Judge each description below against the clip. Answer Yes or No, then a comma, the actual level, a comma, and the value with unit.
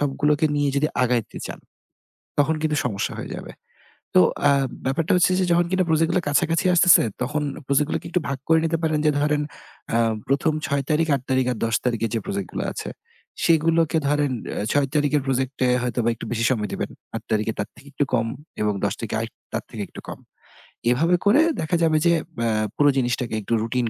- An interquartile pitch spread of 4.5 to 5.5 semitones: Yes, average, 4.8 semitones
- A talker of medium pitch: Yes, medium, 145 Hz